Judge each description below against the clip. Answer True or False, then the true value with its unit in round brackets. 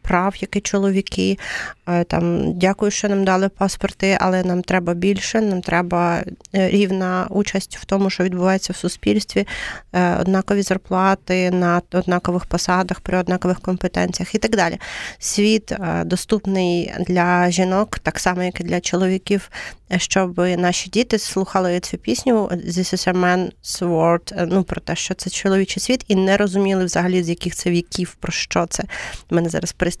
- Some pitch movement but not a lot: False (1.6 semitones)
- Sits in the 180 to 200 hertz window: True (185 Hz)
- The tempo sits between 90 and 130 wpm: False (150 wpm)